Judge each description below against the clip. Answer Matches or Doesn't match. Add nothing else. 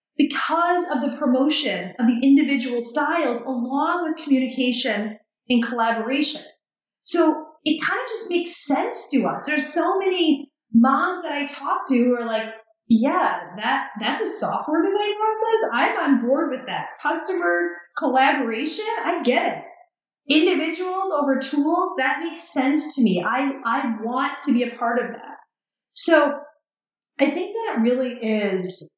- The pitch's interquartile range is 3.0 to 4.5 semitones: Doesn't match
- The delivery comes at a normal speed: Matches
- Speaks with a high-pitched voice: Matches